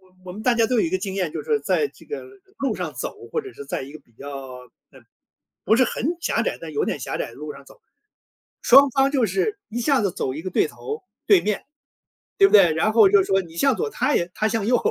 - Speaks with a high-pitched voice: Yes, high, 215 Hz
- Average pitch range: No, wide, 7.8 semitones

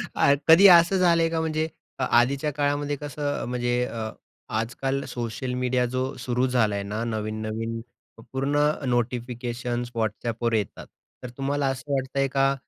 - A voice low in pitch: Yes, low, 125 Hz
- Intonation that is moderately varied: Yes, average, 3.2 semitones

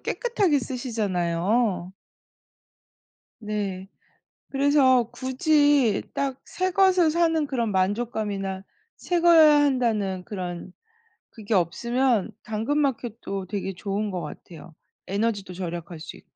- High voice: Yes, high, 220 Hz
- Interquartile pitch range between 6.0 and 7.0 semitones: Yes, wide, 6.5 semitones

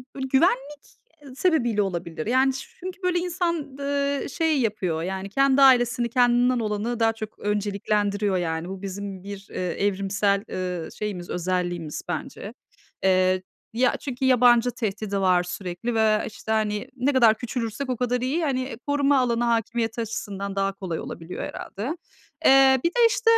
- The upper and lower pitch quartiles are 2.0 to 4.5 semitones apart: No, average, 5.1 semitones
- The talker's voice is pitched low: No, high, 225 Hz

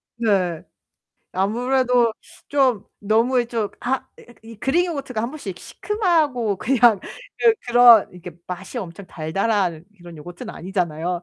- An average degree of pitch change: No, wide, 5.7 semitones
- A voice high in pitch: Yes, high, 225 Hz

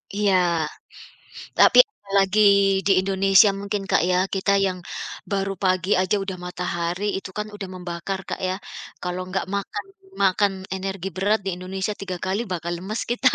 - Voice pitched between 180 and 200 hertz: Yes, high, 190 Hz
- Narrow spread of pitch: Yes, narrow, 1.4 semitones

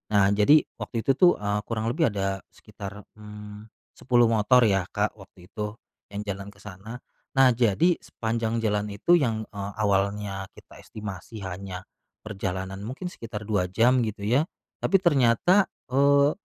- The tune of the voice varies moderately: Yes, average, 3.2 semitones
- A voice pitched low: Yes, low, 105 Hz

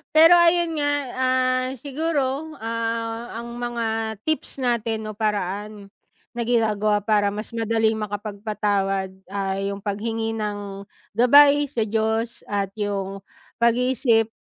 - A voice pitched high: Yes, high, 225 Hz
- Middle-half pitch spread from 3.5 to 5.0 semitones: No, average, 3.0 semitones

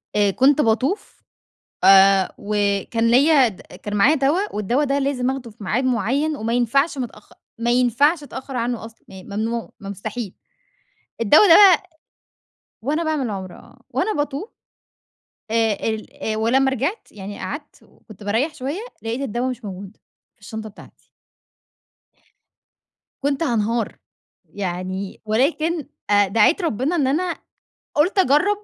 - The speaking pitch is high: Yes, high, 245 Hz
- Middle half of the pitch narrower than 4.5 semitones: No, average, 5.3 semitones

